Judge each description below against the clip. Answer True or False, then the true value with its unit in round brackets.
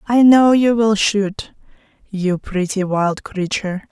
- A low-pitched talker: False (205 Hz)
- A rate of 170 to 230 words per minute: False (140 wpm)